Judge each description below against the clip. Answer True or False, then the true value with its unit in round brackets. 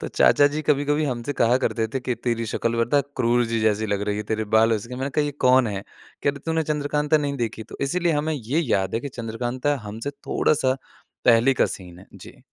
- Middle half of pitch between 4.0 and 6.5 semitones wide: True (4.3 semitones)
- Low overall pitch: True (125 Hz)